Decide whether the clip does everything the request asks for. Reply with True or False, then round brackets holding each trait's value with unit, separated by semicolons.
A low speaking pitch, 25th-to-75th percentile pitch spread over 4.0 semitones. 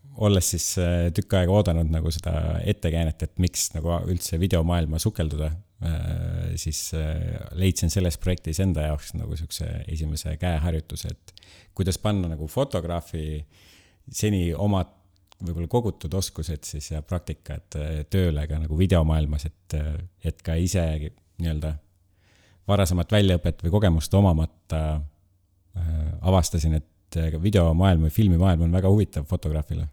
False (85 Hz; 3.0 semitones)